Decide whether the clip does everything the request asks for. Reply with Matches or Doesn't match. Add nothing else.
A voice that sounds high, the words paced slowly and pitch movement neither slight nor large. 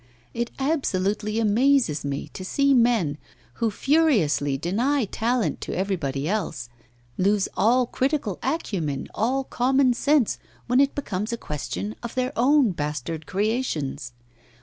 Doesn't match